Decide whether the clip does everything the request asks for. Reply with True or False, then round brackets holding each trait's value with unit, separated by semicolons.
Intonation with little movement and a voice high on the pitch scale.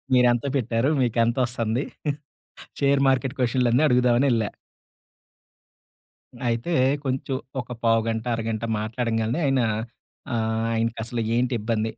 False (1.9 semitones; 120 Hz)